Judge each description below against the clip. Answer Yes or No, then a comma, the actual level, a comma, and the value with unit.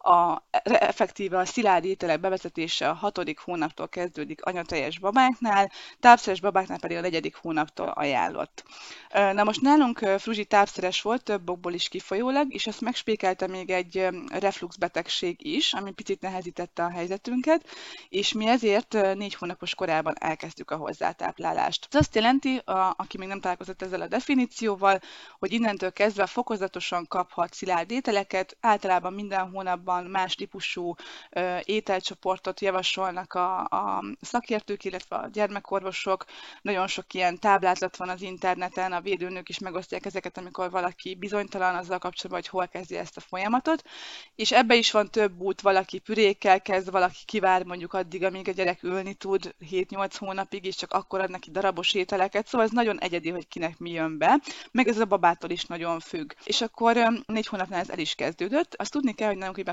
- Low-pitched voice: No, high, 190 Hz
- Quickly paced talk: Yes, fast, 160 wpm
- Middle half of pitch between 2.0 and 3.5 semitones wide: Yes, average, 2.8 semitones